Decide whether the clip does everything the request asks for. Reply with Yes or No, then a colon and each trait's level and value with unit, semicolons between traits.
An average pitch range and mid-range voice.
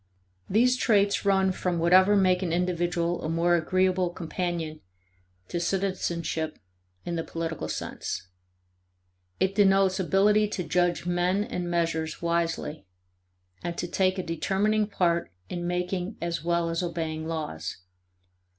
No: narrow, 2.2 semitones; medium, 175 Hz